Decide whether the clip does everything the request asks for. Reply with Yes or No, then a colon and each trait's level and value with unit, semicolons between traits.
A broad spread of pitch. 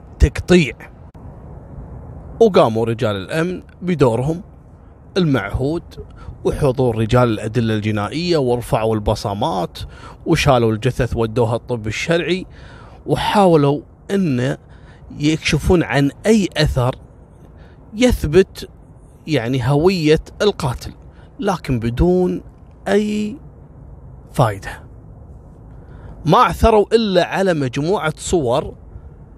Yes: wide, 7.2 semitones